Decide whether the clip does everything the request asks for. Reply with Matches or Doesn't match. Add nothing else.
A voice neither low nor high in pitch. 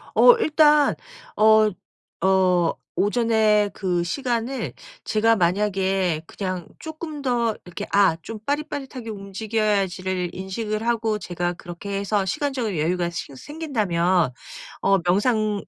Doesn't match